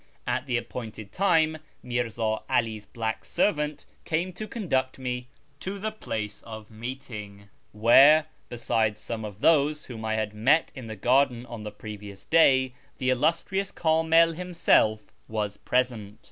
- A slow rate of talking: No, average, 145 wpm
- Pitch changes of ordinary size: No, wide, 6.0 semitones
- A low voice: Yes, low, 125 Hz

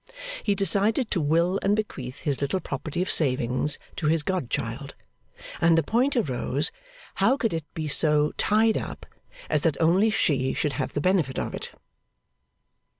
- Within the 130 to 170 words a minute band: Yes, average, 160 wpm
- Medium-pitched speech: Yes, medium, 165 Hz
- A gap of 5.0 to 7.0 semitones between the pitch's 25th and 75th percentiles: Yes, wide, 5.4 semitones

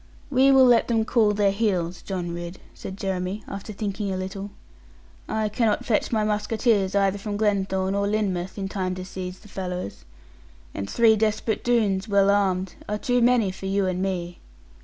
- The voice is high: Yes, high, 200 Hz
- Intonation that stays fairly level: Yes, narrow, 2.3 semitones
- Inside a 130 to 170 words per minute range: No, average, 180 wpm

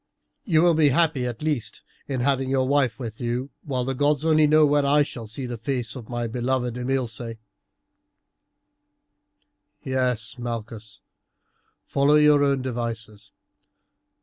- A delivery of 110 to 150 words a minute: Yes, average, 140 wpm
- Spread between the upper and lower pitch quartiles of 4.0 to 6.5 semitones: No, average, 3.3 semitones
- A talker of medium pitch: No, low, 130 Hz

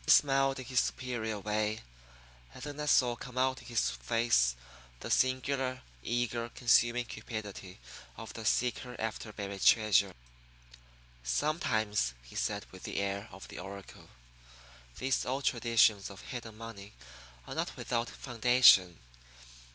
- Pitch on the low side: Yes, low, 115 Hz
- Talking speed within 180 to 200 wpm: No, slow, 135 wpm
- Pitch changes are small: No, average, 3.9 semitones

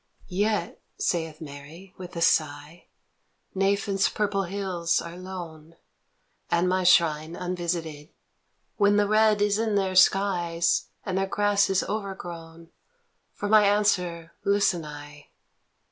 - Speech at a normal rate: No, slow, 130 wpm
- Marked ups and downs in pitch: No, average, 3.3 semitones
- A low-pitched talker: No, medium, 180 Hz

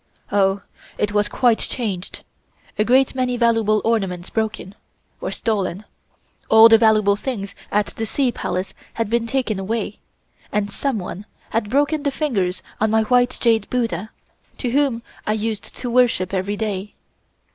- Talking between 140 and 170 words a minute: Yes, average, 150 wpm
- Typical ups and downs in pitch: Yes, average, 3.1 semitones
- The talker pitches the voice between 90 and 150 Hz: No, high, 220 Hz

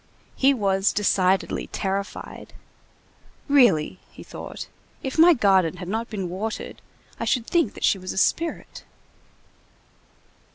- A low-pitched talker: No, high, 200 Hz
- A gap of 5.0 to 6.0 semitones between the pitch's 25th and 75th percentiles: Yes, average, 5.3 semitones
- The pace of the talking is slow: Yes, slow, 125 wpm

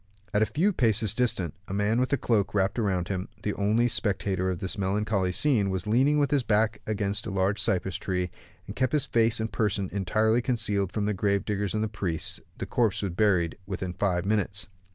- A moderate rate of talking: No, fast, 210 wpm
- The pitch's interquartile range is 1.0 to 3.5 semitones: Yes, average, 2.7 semitones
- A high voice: No, low, 105 Hz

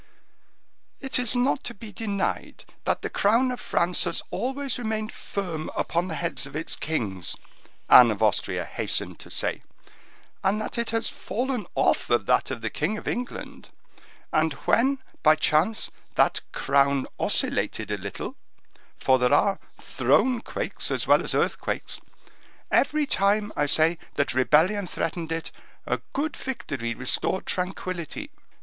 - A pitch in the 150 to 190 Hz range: Yes, medium, 185 Hz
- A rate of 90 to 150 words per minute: Yes, average, 145 wpm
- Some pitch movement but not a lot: No, wide, 7.7 semitones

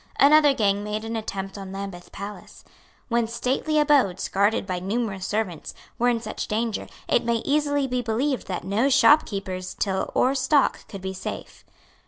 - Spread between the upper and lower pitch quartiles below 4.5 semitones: No, average, 4.8 semitones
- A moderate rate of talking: Yes, average, 165 wpm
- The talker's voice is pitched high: Yes, high, 220 Hz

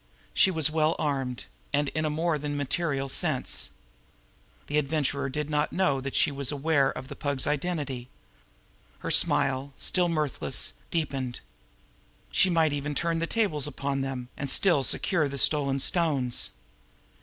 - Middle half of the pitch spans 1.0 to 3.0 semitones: Yes, narrow, 2.6 semitones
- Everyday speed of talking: Yes, average, 150 wpm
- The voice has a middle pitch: Yes, medium, 145 Hz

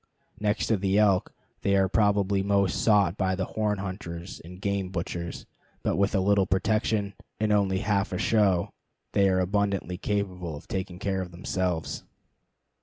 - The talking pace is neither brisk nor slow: Yes, average, 165 wpm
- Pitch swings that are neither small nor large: No, narrow, 1.8 semitones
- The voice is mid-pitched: No, very low, 95 Hz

